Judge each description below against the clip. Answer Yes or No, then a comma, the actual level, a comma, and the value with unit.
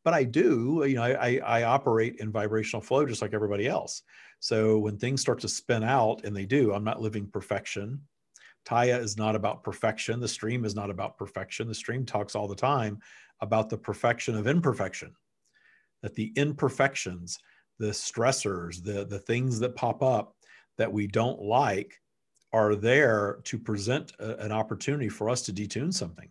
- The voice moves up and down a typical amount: Yes, average, 3.1 semitones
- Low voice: Yes, low, 110 Hz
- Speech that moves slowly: No, average, 180 wpm